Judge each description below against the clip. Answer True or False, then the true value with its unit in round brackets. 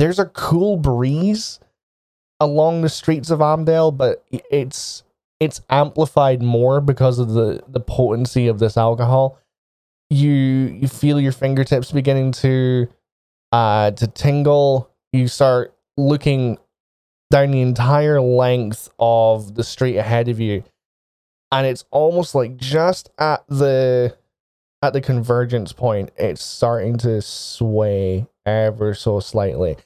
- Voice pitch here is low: True (130 Hz)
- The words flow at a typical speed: False (125 wpm)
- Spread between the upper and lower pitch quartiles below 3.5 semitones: False (3.8 semitones)